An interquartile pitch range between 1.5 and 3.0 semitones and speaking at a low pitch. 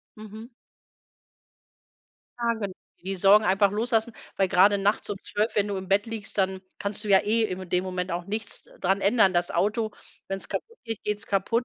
No: narrow, 2.4 semitones; high, 200 Hz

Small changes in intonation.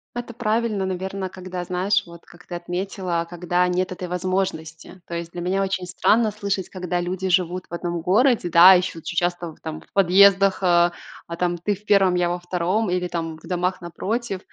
Yes: narrow, 1.8 semitones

